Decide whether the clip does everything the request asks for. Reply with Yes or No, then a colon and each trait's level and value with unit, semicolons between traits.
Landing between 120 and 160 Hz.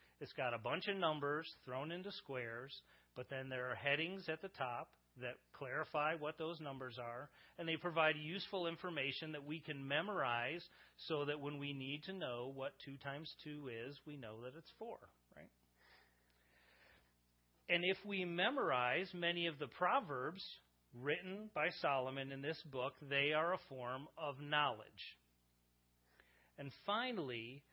Yes: medium, 140 Hz